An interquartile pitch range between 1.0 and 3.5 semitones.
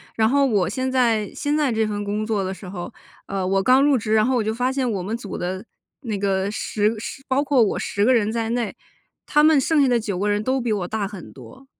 No: average, 4.2 semitones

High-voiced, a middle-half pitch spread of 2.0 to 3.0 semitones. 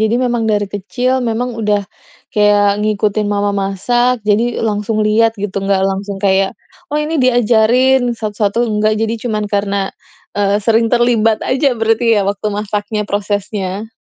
Yes: high, 215 Hz; narrow, 2.4 semitones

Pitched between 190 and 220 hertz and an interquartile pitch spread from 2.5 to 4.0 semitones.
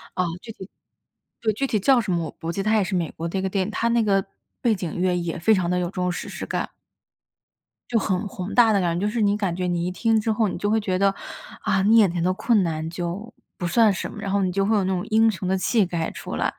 Yes: high, 195 Hz; average, 3.2 semitones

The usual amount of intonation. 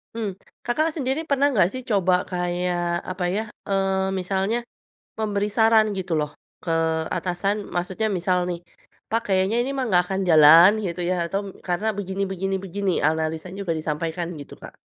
Yes: average, 3.0 semitones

